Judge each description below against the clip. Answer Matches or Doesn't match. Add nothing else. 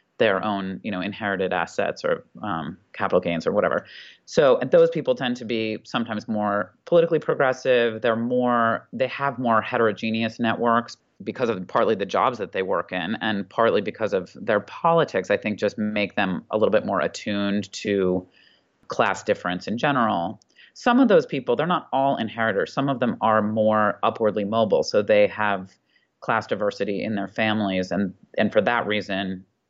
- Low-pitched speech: Matches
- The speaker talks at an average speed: Matches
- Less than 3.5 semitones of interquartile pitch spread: Doesn't match